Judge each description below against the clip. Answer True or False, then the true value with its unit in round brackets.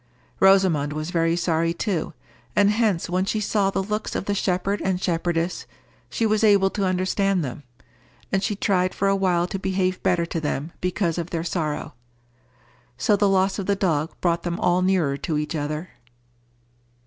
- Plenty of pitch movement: False (2.8 semitones)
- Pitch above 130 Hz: True (185 Hz)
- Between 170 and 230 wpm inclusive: True (180 wpm)